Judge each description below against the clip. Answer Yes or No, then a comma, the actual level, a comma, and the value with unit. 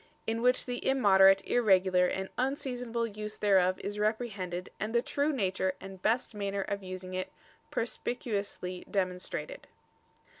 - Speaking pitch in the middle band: No, high, 200 Hz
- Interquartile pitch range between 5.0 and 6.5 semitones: No, average, 4.0 semitones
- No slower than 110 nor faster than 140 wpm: Yes, slow, 135 wpm